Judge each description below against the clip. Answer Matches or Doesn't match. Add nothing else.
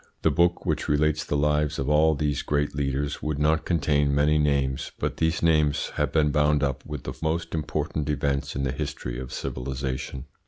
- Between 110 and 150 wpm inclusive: Doesn't match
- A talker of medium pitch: Doesn't match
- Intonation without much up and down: Matches